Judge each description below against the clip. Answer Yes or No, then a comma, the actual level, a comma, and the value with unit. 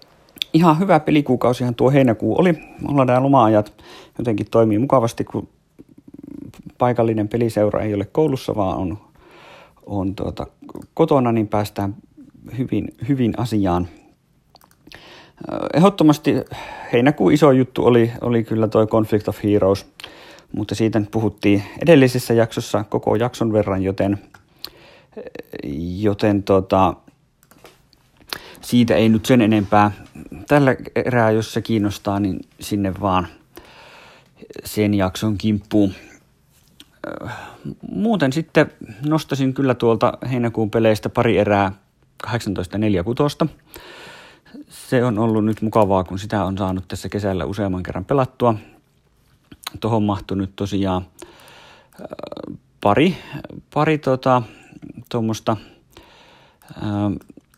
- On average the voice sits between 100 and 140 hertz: Yes, low, 110 Hz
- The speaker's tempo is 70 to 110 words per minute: Yes, average, 100 wpm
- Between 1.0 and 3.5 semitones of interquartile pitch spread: No, average, 3.9 semitones